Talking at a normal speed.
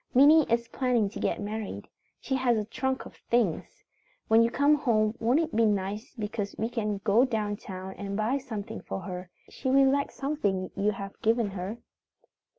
Yes: average, 185 wpm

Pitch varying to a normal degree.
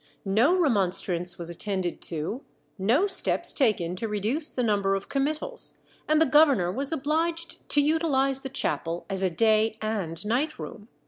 No: wide, 7.4 semitones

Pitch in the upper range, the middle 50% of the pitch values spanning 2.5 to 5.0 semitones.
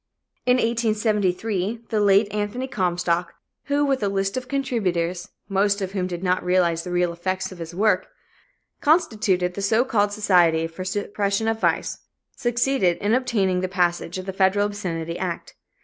Yes: high, 195 Hz; average, 3.5 semitones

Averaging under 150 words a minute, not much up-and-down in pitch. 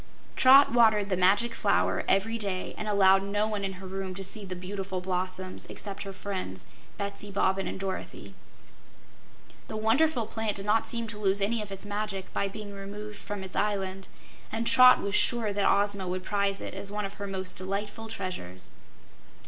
No: average, 185 wpm; narrow, 1.8 semitones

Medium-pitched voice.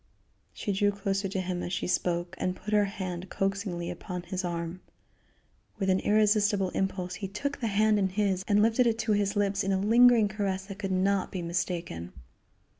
No: high, 195 Hz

